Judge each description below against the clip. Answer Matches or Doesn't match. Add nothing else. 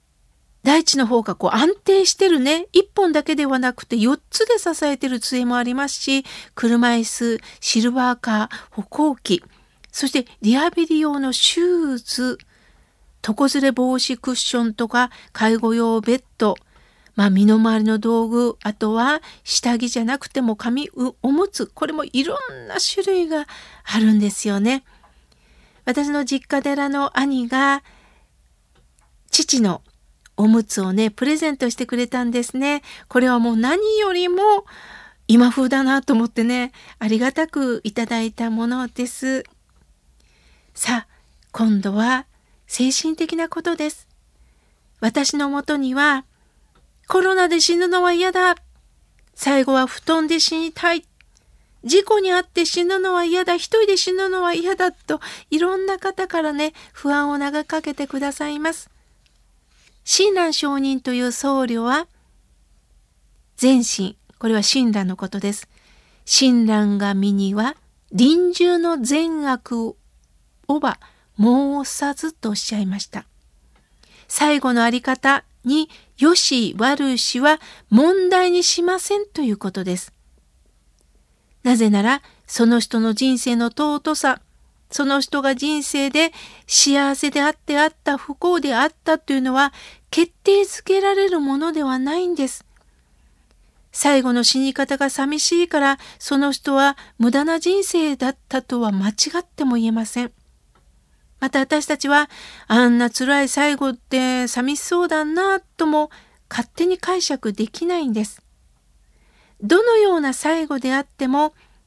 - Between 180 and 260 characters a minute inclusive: Matches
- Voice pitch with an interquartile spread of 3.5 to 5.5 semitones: Matches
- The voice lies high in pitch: Matches